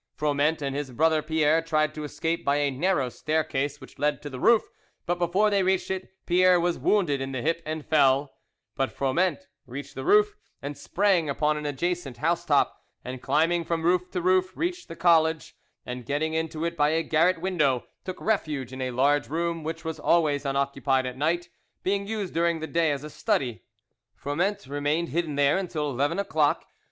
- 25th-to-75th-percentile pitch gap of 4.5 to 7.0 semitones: No, average, 3.5 semitones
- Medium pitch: Yes, medium, 160 Hz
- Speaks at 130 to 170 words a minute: No, average, 190 wpm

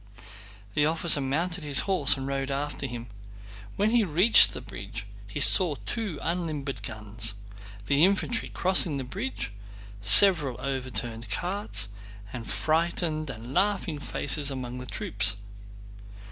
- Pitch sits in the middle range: Yes, medium, 145 Hz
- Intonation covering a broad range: Yes, wide, 5.9 semitones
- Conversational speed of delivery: No, slow, 130 wpm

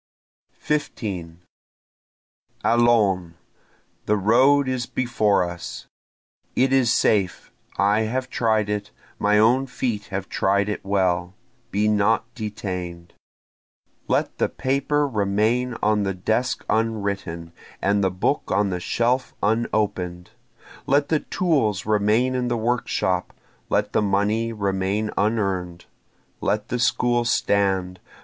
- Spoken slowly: Yes, slow, 115 wpm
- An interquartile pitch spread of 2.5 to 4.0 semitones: Yes, average, 3.6 semitones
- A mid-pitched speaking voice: No, low, 105 Hz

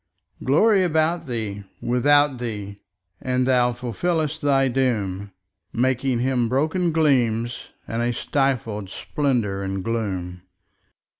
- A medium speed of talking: No, slow, 100 wpm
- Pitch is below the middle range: Yes, low, 125 Hz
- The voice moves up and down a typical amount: Yes, average, 5.0 semitones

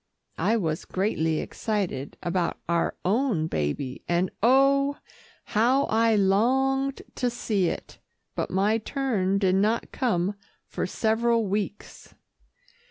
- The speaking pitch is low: No, high, 210 Hz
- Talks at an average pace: No, slow, 115 wpm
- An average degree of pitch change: Yes, average, 4.7 semitones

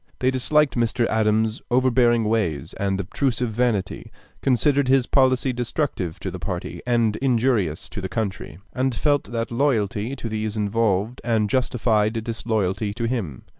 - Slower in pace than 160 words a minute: Yes, average, 145 wpm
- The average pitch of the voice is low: Yes, low, 115 Hz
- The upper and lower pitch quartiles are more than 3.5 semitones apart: No, average, 3.2 semitones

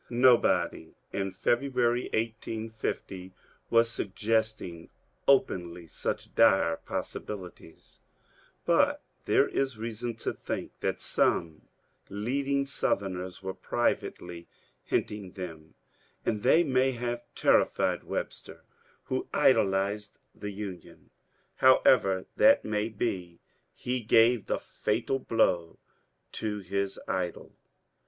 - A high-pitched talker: No, low, 105 Hz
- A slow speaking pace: Yes, slow, 100 wpm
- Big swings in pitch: No, average, 4.3 semitones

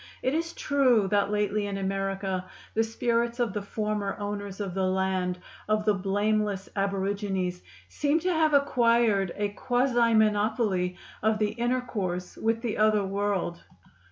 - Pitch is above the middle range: Yes, high, 210 Hz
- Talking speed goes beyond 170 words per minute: No, average, 145 wpm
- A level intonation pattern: No, average, 3.0 semitones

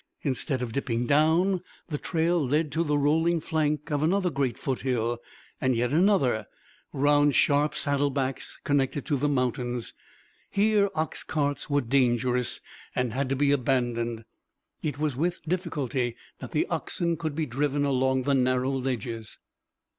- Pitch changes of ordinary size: Yes, average, 3.4 semitones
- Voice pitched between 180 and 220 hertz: No, medium, 140 Hz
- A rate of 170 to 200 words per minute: No, average, 145 wpm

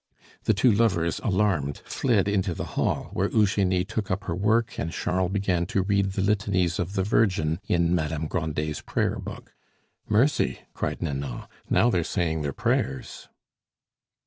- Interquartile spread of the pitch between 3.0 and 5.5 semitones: Yes, average, 3.8 semitones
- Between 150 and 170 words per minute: Yes, average, 155 wpm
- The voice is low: Yes, very low, 95 Hz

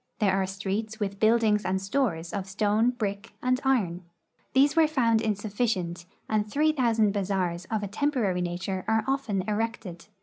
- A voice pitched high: Yes, high, 210 Hz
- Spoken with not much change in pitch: No, average, 3.4 semitones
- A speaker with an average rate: Yes, average, 160 wpm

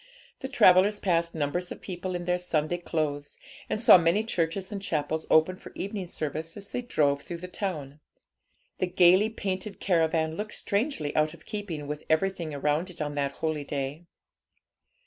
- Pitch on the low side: No, medium, 170 Hz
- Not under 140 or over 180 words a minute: Yes, average, 170 wpm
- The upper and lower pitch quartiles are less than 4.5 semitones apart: Yes, average, 3.7 semitones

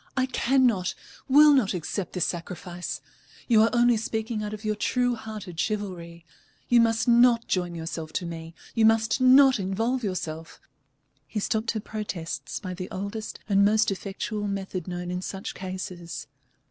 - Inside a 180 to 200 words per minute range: No, average, 160 wpm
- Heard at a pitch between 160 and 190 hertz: No, high, 205 Hz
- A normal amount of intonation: Yes, average, 4.1 semitones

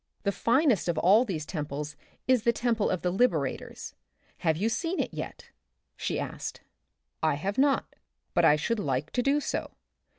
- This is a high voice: Yes, high, 200 Hz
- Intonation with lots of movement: Yes, wide, 7.6 semitones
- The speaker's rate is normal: Yes, average, 175 wpm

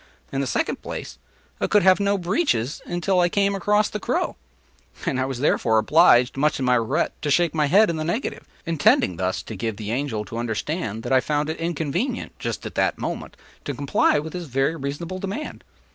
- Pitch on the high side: No, medium, 150 Hz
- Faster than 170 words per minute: Yes, average, 200 wpm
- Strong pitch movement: Yes, wide, 6.1 semitones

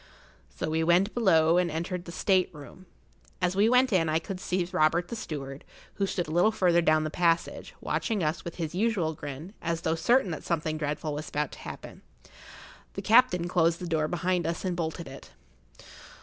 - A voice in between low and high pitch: Yes, medium, 170 Hz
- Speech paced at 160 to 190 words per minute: No, average, 200 wpm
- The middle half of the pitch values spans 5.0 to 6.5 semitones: No, average, 2.7 semitones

